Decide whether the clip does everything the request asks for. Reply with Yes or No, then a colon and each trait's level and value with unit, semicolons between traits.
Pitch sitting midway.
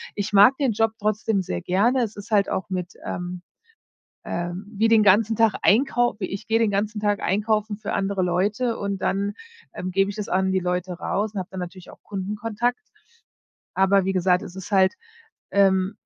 No: high, 200 Hz